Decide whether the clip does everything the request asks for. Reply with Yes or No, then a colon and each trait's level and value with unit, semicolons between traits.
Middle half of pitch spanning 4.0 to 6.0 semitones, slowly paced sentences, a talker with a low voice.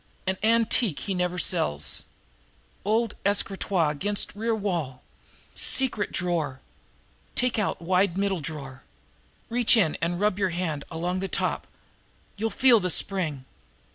No: average, 4.3 semitones; slow, 130 wpm; medium, 185 Hz